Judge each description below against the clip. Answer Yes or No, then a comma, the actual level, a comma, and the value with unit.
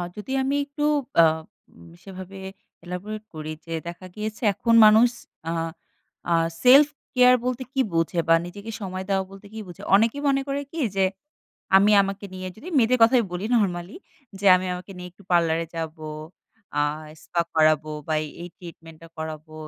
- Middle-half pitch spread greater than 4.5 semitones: Yes, average, 5.2 semitones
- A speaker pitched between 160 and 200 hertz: Yes, high, 190 Hz